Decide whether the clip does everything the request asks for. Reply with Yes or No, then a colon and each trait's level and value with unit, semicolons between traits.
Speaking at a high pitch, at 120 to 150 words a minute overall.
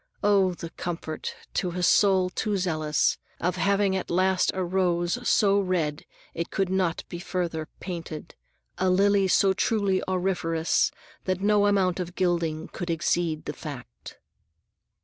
No: medium, 180 Hz; average, 145 wpm